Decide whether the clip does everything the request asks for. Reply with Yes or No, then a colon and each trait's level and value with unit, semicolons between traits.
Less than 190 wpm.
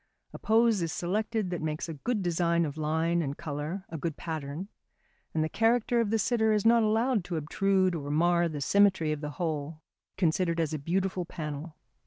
No: average, 195 wpm